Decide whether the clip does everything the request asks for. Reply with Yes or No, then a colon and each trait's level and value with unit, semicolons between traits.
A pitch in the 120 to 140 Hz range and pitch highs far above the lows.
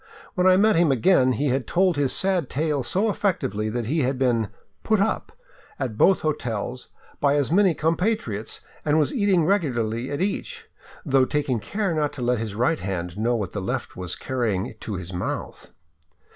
Yes: low, 135 Hz; wide, 7.8 semitones